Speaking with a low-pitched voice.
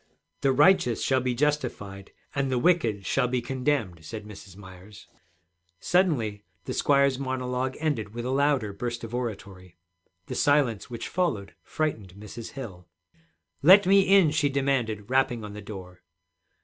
Yes: low, 125 Hz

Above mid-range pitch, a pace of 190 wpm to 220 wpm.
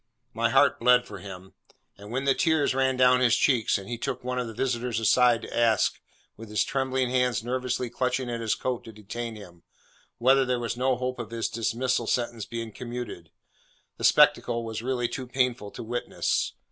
No: low, 120 Hz; average, 195 wpm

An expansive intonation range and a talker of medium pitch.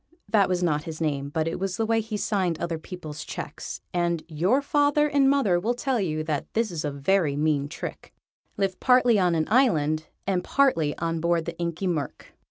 Yes: wide, 5.9 semitones; medium, 175 Hz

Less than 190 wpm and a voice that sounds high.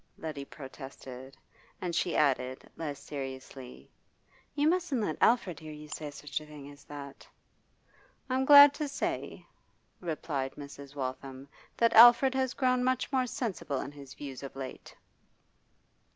No: average, 140 wpm; medium, 150 Hz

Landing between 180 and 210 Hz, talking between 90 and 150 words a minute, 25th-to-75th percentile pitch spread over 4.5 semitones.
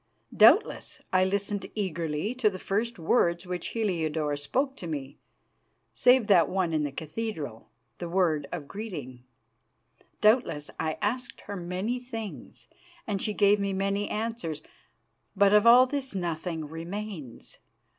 Yes: high, 190 Hz; slow, 135 wpm; average, 5.2 semitones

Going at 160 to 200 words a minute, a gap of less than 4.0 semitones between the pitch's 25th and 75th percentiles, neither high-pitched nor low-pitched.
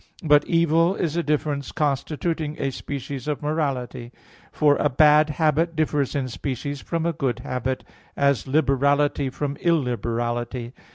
No: slow, 135 wpm; average, 2.8 semitones; medium, 145 Hz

